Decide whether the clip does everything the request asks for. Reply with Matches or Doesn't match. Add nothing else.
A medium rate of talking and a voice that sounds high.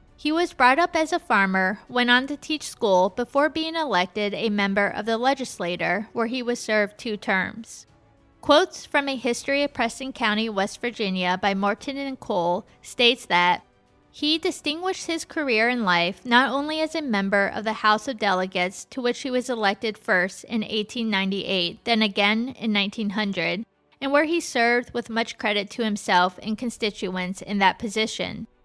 Matches